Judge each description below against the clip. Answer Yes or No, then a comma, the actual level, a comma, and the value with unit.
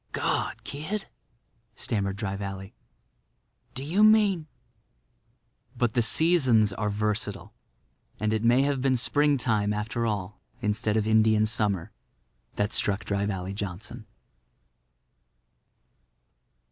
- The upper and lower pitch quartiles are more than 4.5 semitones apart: No, average, 4.0 semitones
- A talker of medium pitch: No, low, 110 Hz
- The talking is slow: Yes, slow, 110 wpm